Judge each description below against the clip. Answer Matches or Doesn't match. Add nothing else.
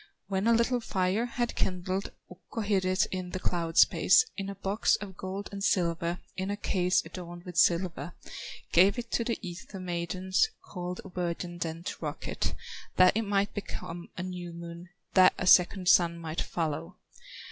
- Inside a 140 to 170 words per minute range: Doesn't match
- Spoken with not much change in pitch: Matches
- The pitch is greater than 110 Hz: Matches